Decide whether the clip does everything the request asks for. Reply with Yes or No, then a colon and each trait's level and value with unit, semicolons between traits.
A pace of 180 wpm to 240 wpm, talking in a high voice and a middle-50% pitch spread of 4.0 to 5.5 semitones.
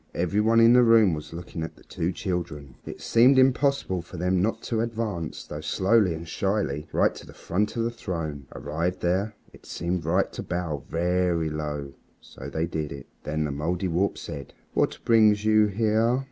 No: average, 190 wpm; very low, 90 Hz; average, 5.2 semitones